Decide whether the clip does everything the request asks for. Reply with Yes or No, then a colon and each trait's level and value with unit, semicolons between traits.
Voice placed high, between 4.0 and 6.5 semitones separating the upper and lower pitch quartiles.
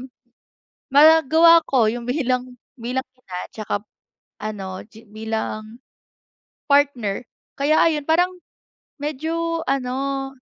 Yes: very high, 260 Hz; average, 5.2 semitones